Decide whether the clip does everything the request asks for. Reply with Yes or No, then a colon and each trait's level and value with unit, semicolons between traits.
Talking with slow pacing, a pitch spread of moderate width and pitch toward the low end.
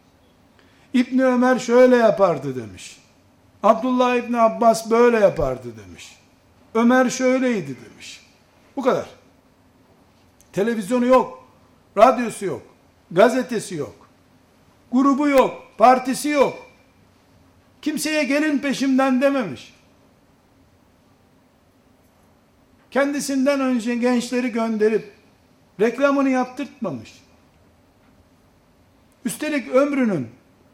No: slow, 75 wpm; average, 4.1 semitones; high, 245 Hz